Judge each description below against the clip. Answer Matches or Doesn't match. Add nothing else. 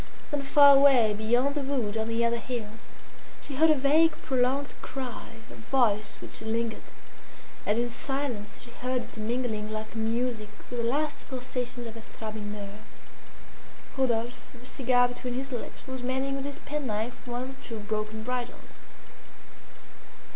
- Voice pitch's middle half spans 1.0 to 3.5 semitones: Matches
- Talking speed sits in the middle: Matches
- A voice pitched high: Matches